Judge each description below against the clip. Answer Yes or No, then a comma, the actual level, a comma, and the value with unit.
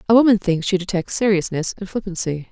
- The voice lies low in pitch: No, high, 190 Hz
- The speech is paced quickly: No, average, 190 wpm